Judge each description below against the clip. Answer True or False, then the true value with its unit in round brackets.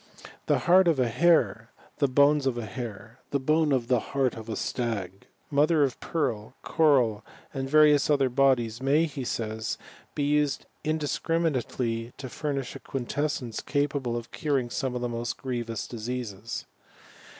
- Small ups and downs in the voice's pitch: False (3.9 semitones)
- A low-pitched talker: True (130 Hz)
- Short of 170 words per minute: True (160 wpm)